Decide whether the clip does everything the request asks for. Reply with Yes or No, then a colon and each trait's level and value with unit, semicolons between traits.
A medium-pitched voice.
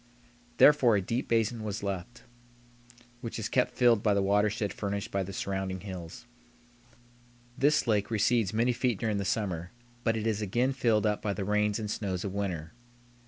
No: low, 105 Hz